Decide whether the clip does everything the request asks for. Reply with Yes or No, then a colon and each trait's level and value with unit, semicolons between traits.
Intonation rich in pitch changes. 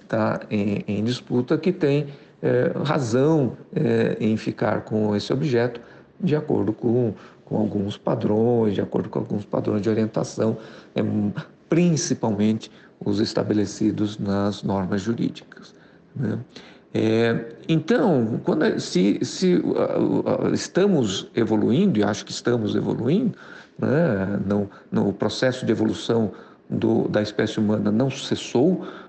No: average, 3.8 semitones